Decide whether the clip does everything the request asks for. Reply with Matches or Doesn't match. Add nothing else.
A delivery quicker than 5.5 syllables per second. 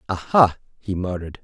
Matches